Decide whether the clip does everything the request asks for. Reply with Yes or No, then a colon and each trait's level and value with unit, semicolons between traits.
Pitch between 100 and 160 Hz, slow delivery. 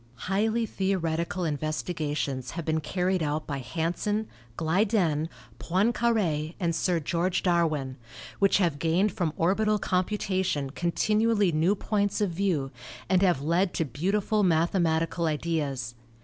No: medium, 170 Hz; slow, 120 wpm